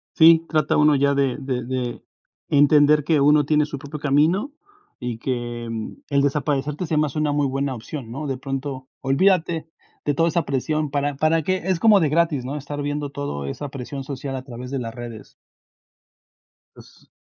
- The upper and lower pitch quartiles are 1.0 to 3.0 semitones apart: Yes, narrow, 2.4 semitones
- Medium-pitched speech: Yes, medium, 145 Hz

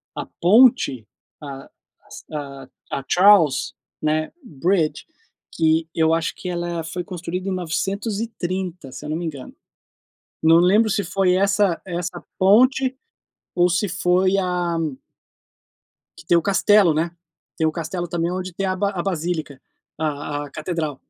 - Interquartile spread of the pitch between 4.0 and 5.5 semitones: No, average, 3.0 semitones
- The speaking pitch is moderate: Yes, medium, 175 Hz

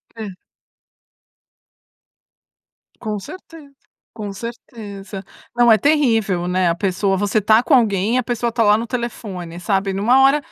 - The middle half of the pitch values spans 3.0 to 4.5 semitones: Yes, average, 3.6 semitones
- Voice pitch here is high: Yes, high, 215 Hz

